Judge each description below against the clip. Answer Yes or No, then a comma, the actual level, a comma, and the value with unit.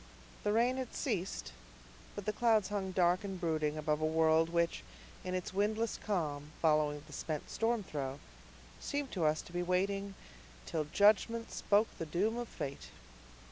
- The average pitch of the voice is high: No, medium, 180 Hz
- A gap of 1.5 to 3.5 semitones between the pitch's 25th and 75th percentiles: No, average, 5.1 semitones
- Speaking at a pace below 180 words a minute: Yes, average, 165 wpm